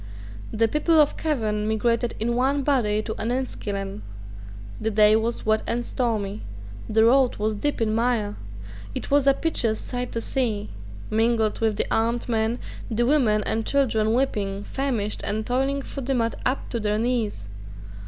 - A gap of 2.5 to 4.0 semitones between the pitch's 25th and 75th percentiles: Yes, average, 2.9 semitones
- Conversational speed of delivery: Yes, average, 165 wpm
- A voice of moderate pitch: No, high, 230 Hz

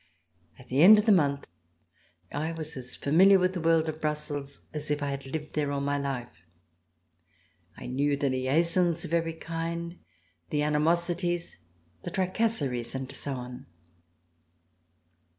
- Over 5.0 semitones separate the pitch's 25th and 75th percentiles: No, average, 3.3 semitones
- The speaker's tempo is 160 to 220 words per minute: No, average, 150 wpm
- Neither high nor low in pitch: Yes, medium, 150 Hz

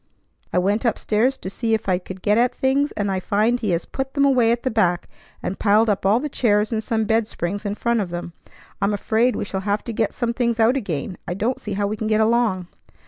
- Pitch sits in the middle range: No, high, 215 Hz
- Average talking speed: No, fast, 250 wpm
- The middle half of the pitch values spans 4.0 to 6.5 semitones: No, average, 3.0 semitones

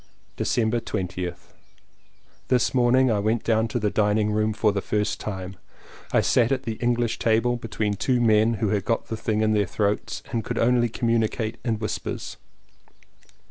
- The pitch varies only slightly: Yes, narrow, 2.0 semitones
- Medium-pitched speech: No, low, 110 Hz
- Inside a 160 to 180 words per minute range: Yes, average, 170 wpm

